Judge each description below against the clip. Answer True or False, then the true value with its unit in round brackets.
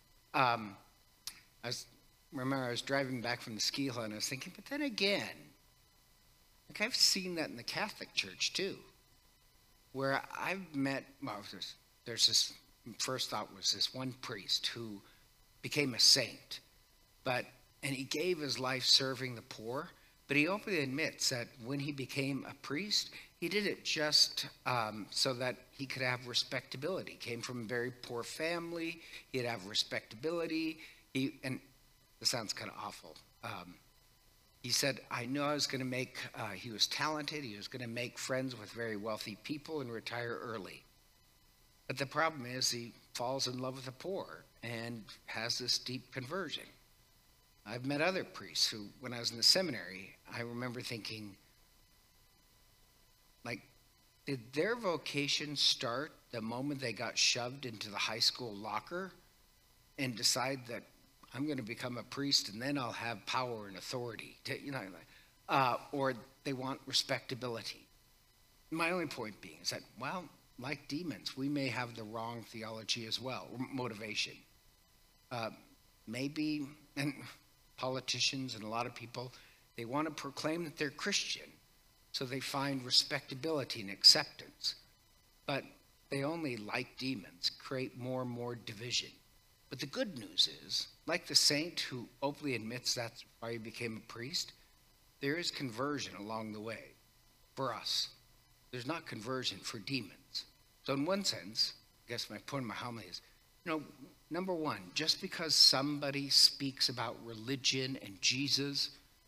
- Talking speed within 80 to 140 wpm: False (160 wpm)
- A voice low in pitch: True (130 Hz)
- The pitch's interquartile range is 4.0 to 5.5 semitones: False (3.3 semitones)